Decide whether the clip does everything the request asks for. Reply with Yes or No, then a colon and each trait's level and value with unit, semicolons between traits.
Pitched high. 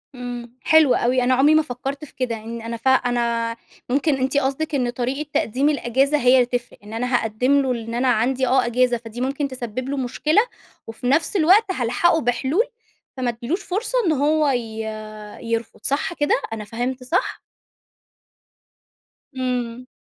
Yes: very high, 255 Hz